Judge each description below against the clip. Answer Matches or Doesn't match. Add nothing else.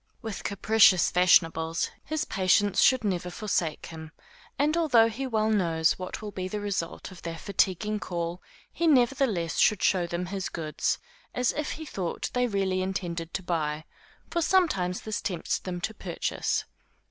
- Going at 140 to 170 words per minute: Matches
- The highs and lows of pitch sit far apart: Doesn't match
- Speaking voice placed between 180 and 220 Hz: Matches